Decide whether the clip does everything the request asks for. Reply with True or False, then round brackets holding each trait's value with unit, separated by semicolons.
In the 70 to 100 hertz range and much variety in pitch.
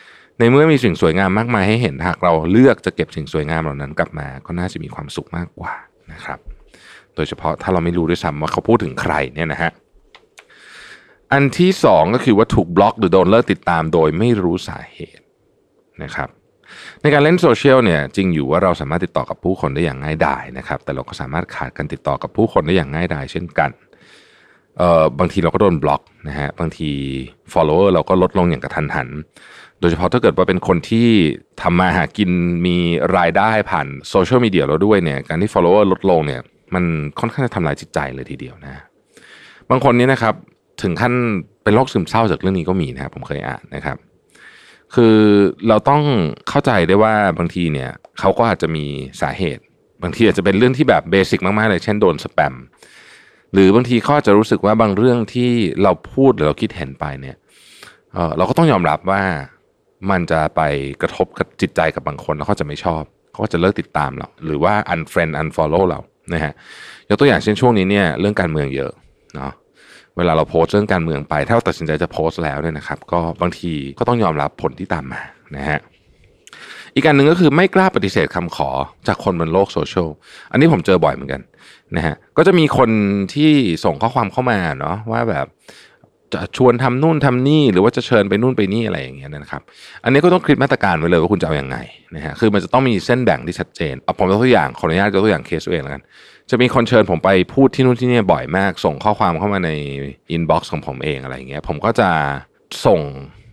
True (95 Hz; 6.4 semitones)